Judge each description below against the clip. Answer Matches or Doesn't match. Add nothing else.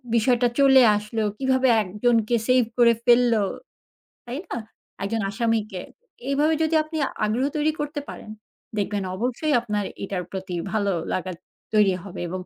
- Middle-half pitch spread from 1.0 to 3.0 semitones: Doesn't match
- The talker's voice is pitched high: Matches